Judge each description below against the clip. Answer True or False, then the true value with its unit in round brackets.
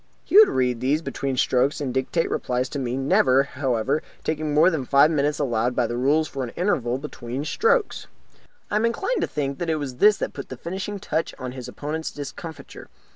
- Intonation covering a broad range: False (3.9 semitones)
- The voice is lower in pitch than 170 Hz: True (140 Hz)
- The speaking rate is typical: False (215 wpm)